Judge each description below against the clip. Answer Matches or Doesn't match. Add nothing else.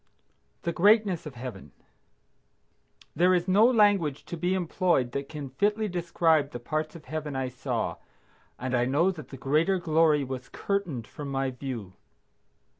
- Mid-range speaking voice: Matches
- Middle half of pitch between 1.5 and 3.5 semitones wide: Doesn't match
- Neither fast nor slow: Matches